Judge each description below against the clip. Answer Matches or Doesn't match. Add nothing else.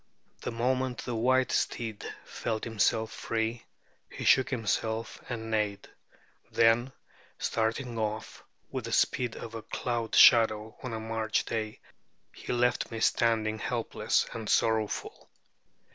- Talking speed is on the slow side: Matches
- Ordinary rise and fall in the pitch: Doesn't match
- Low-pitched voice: Matches